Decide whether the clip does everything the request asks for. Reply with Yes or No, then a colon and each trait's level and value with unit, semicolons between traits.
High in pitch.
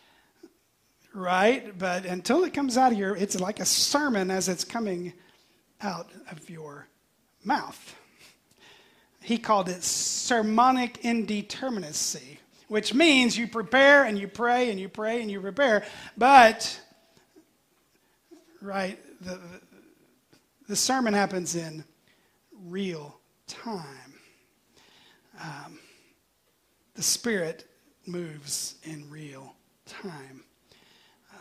Yes: high, 200 Hz